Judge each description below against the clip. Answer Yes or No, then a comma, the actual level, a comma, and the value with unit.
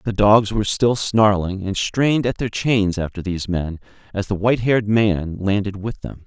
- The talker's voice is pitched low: Yes, low, 105 Hz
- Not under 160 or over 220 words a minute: Yes, average, 200 wpm